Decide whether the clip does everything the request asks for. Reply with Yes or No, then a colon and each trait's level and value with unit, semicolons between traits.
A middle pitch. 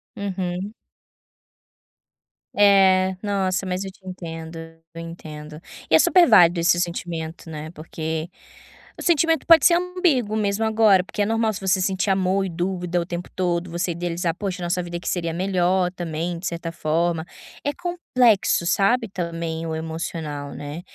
Yes: medium, 180 Hz